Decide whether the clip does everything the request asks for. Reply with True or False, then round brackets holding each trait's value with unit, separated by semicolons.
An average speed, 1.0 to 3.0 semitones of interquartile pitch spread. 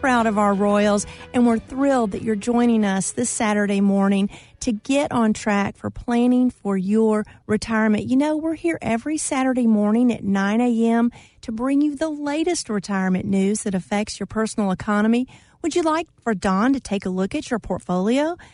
False (185 wpm; 3.7 semitones)